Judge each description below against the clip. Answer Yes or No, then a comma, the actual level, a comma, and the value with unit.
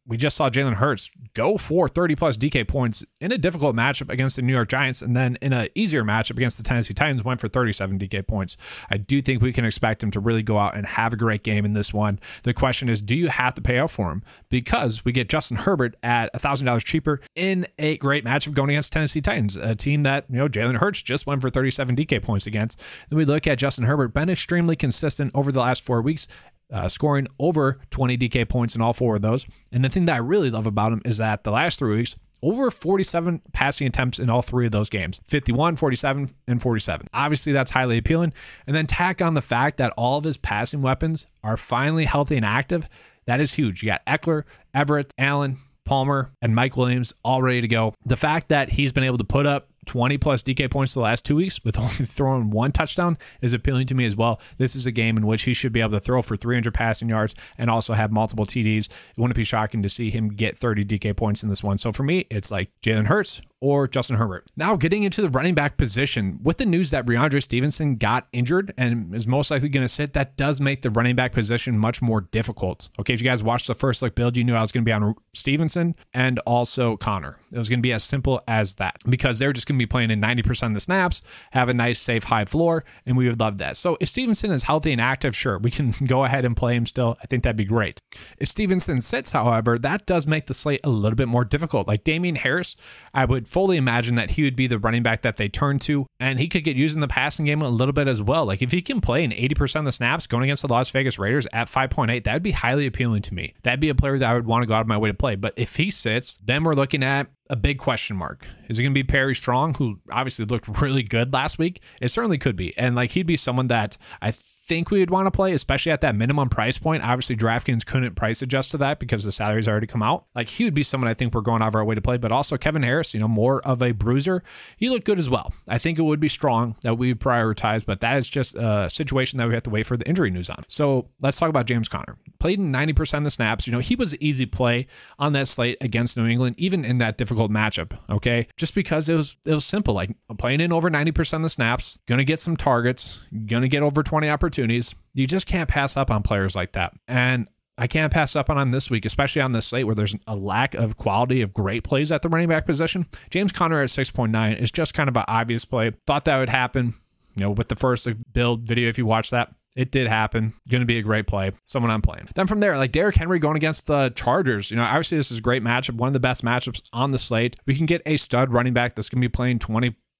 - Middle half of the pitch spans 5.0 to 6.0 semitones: No, average, 4.1 semitones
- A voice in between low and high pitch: No, low, 125 Hz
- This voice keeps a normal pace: No, fast, 260 wpm